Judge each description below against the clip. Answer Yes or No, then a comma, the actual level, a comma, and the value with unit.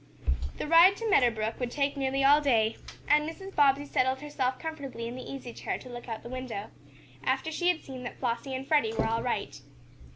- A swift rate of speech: Yes, fast, 220 wpm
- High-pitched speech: Yes, very high, 265 Hz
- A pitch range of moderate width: Yes, average, 3.6 semitones